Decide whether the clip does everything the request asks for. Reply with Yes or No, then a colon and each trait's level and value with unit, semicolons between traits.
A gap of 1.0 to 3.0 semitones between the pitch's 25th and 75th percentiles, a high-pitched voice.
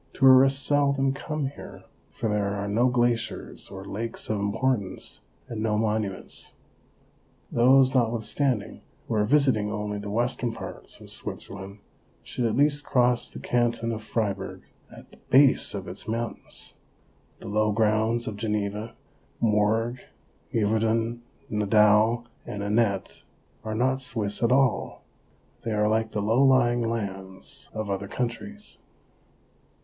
No: average, 2.7 semitones; low, 115 Hz